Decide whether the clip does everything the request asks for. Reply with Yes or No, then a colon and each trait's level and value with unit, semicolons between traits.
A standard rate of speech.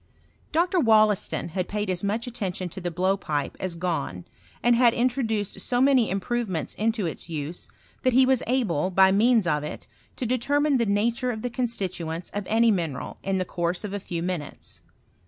Yes: average, 185 wpm